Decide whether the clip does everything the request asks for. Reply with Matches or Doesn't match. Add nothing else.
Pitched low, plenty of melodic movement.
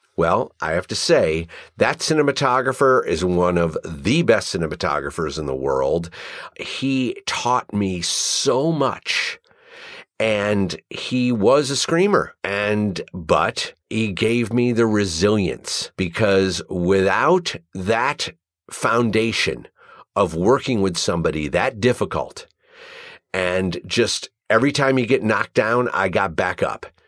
Matches